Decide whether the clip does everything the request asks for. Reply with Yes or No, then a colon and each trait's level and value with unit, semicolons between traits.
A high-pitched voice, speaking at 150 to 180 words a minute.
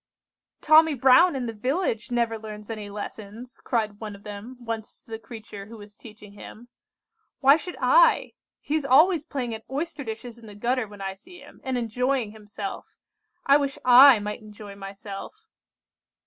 Yes: high, 230 Hz; average, 175 wpm